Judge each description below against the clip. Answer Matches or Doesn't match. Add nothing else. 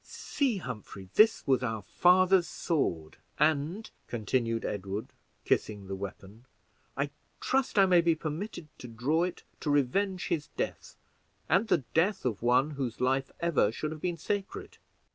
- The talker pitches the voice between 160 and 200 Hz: Doesn't match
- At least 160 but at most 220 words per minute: Doesn't match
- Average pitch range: Doesn't match